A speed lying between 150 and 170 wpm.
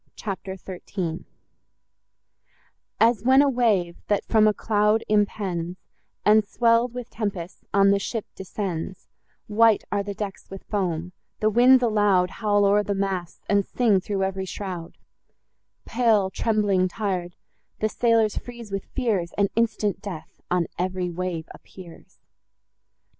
No: slow, 135 wpm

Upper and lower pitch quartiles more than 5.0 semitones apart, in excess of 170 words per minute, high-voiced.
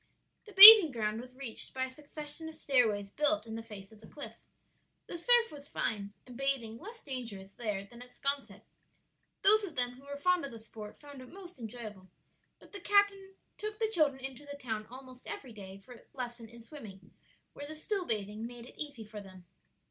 Yes: wide, 5.5 semitones; fast, 205 wpm; very high, 255 Hz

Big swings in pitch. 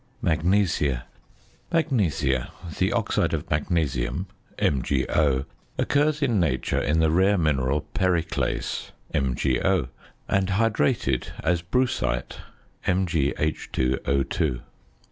Yes: wide, 5.8 semitones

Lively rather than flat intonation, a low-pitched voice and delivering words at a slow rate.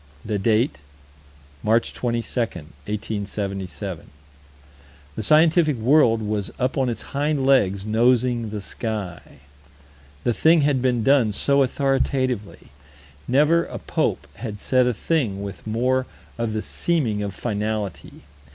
No: average, 4.2 semitones; low, 115 Hz; slow, 125 wpm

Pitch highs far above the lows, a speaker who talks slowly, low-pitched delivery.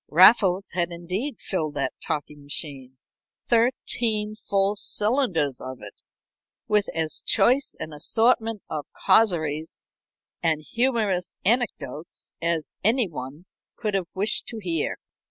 No: wide, 6.2 semitones; slow, 120 wpm; medium, 185 Hz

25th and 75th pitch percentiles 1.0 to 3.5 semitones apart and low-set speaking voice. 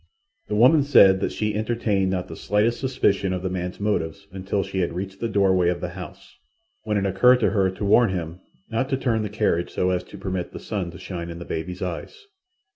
Yes: average, 2.9 semitones; very low, 95 Hz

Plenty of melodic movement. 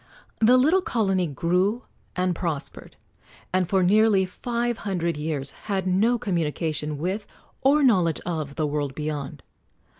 Yes: wide, 5.8 semitones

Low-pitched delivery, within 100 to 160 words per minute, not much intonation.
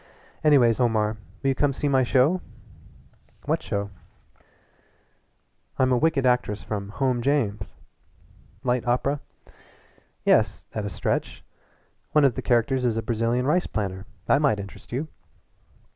No: low, 125 Hz; average, 140 wpm; average, 4.0 semitones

